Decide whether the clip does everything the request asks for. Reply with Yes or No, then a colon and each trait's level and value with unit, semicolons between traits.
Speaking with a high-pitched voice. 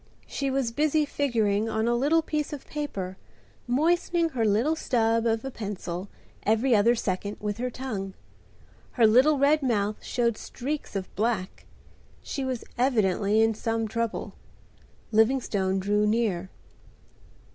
Yes: high, 230 Hz